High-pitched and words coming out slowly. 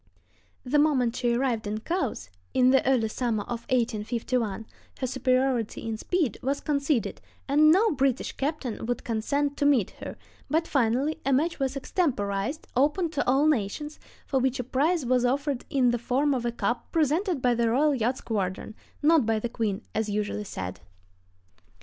No: very high, 255 Hz; average, 170 wpm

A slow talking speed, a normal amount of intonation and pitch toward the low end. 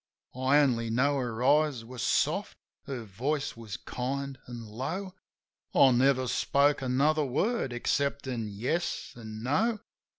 Yes: slow, 130 wpm; average, 3.2 semitones; low, 130 Hz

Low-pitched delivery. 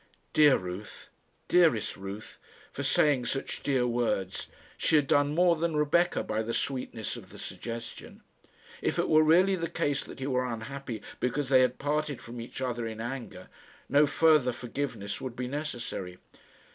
Yes: low, 130 Hz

